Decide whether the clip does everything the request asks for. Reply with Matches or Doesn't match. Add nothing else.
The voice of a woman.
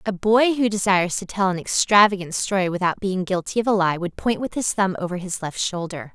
Matches